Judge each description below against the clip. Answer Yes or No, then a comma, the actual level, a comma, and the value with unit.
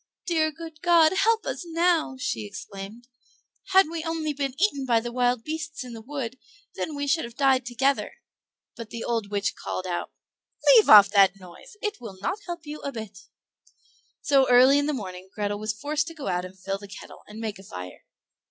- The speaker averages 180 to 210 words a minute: Yes, average, 200 wpm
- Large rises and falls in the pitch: Yes, wide, 7.3 semitones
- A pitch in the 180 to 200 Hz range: No, very high, 255 Hz